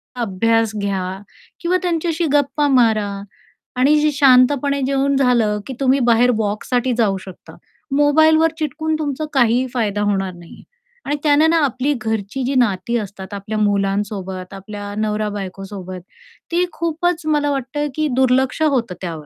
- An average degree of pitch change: No, wide, 6.2 semitones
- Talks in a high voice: Yes, high, 245 Hz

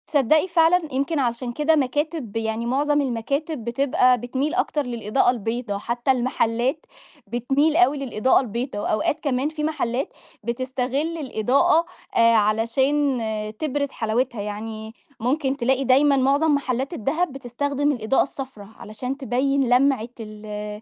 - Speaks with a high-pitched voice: Yes, very high, 260 Hz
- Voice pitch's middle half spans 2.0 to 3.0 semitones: No, average, 3.6 semitones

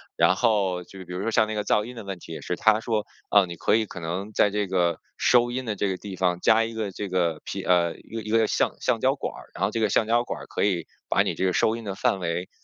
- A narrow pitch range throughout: No, average, 3.5 semitones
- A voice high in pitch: No, low, 100 Hz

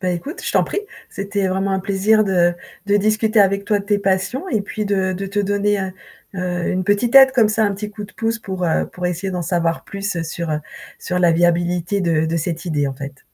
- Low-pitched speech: No, high, 195 Hz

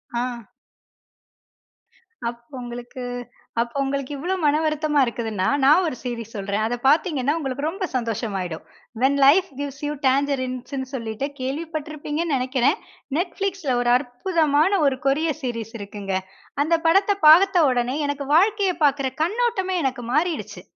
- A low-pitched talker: No, very high, 280 Hz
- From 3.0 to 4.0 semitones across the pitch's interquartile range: No, average, 4.7 semitones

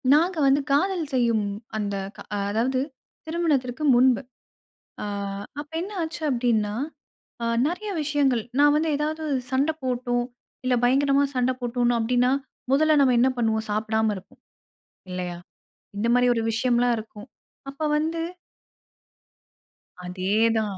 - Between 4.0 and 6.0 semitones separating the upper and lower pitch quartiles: Yes, average, 4.6 semitones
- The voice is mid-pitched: No, very high, 250 Hz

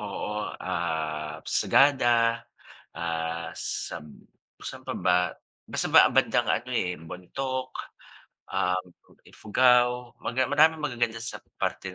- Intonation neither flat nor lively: No, wide, 6.3 semitones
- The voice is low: Yes, low, 110 Hz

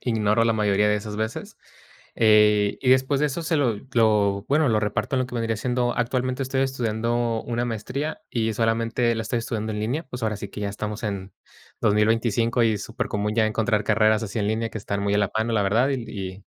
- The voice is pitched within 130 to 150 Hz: No, low, 110 Hz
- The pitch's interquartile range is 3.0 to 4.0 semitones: No, narrow, 2.4 semitones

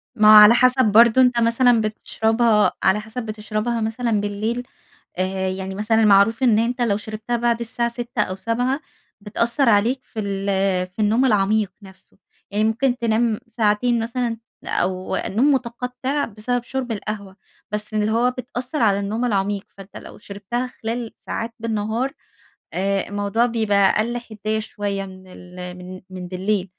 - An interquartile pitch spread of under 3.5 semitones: Yes, average, 2.9 semitones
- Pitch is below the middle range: No, high, 220 Hz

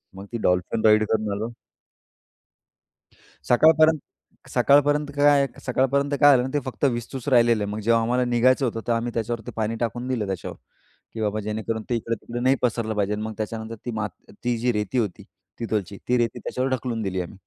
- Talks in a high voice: No, low, 115 Hz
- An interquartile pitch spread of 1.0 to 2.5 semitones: No, average, 2.9 semitones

